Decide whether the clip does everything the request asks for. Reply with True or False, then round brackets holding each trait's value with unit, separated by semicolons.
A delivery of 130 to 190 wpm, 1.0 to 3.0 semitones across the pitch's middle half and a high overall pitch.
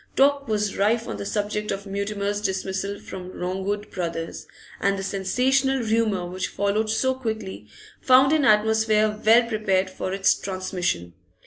True (145 wpm; 2.6 semitones; 205 Hz)